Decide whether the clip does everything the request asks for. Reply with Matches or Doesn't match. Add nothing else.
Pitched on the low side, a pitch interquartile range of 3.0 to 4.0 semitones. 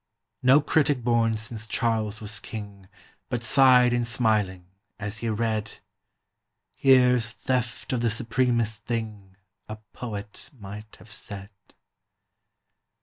Doesn't match